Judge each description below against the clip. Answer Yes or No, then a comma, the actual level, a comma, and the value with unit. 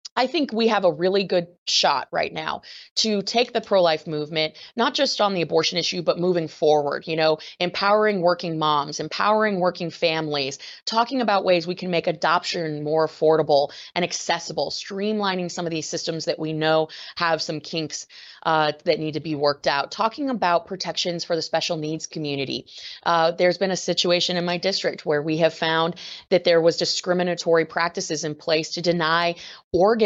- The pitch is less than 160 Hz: No, medium, 170 Hz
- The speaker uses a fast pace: No, average, 180 wpm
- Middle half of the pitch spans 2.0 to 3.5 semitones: Yes, average, 2.7 semitones